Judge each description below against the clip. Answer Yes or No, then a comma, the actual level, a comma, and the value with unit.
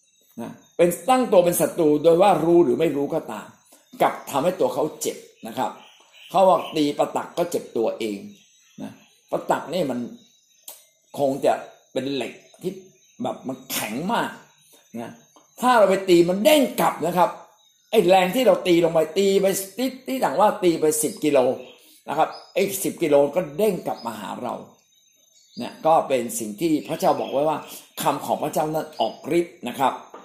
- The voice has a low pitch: No, medium, 175 Hz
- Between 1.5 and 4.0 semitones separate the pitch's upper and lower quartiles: No, average, 5.1 semitones